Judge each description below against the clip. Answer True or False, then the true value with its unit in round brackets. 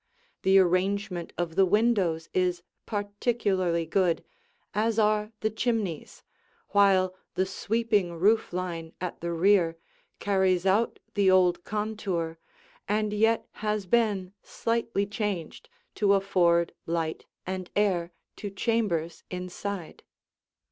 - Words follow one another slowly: True (115 wpm)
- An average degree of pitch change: True (3.2 semitones)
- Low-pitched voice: False (195 Hz)